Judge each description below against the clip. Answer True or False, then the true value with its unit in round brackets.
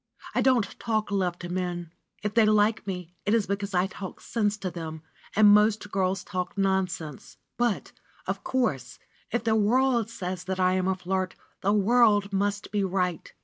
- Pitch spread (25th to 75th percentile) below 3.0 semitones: True (2.6 semitones)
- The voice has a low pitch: False (195 Hz)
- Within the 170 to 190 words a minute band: True (180 wpm)